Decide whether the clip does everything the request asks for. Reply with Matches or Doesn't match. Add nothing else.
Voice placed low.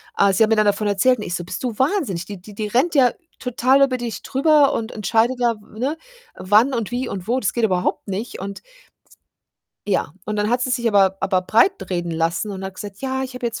Doesn't match